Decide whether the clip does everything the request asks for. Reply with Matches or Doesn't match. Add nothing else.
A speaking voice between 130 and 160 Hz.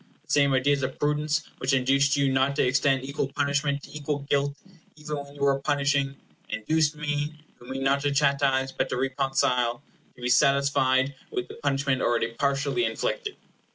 Matches